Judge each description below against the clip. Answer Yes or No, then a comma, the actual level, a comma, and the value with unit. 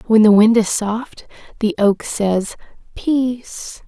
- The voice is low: No, high, 220 Hz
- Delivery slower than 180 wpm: Yes, average, 140 wpm